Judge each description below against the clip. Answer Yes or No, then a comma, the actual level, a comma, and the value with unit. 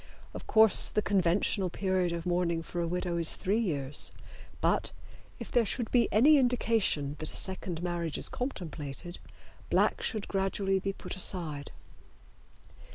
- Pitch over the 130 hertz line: Yes, medium, 185 Hz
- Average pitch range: Yes, average, 3.5 semitones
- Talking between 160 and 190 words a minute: No, average, 150 wpm